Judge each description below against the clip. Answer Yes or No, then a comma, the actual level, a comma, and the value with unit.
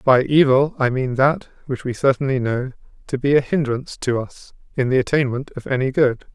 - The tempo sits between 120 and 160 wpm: No, average, 200 wpm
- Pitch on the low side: Yes, low, 130 Hz